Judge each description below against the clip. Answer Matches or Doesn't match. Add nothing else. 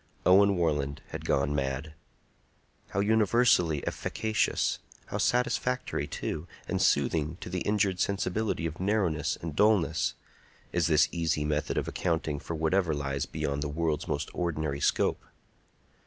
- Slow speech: Matches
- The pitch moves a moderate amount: Matches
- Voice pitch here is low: Matches